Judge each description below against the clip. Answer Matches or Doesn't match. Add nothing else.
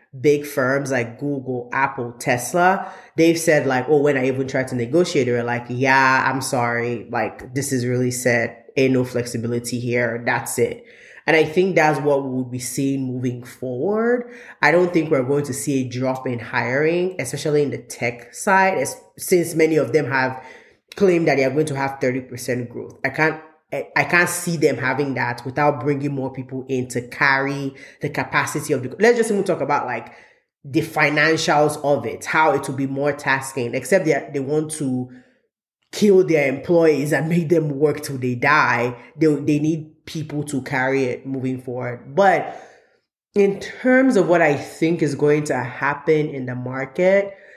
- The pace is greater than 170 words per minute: Matches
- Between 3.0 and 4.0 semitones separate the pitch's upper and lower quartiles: Matches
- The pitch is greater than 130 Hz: Matches